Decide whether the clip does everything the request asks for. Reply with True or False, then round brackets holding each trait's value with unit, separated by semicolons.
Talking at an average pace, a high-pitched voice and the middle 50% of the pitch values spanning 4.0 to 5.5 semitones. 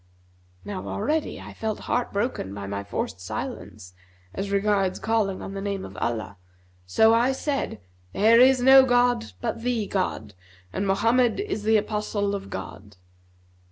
True (155 wpm; 205 Hz; 4.3 semitones)